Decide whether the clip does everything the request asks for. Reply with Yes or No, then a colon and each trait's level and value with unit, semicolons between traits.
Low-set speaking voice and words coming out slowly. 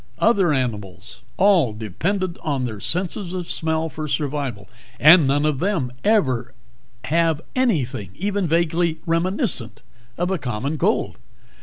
No: medium, 155 Hz; slow, 130 wpm